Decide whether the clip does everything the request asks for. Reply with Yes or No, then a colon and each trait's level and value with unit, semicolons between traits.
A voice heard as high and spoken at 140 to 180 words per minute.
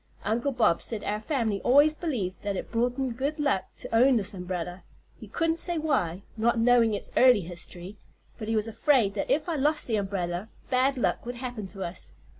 No: high, 230 Hz; fast, 205 wpm